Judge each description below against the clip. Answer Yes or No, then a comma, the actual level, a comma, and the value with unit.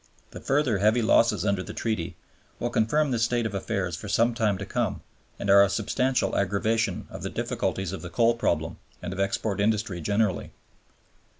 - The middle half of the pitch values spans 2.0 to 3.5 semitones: Yes, average, 3.0 semitones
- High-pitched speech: No, low, 105 Hz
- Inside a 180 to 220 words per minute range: Yes, average, 185 wpm